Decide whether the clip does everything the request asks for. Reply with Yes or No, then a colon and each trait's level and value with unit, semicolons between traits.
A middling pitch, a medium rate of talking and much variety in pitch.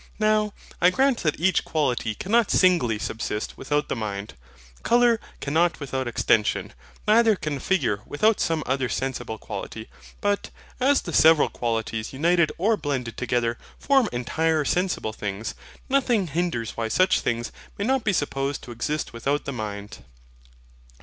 Yes: medium, 145 Hz; average, 145 wpm; wide, 8.4 semitones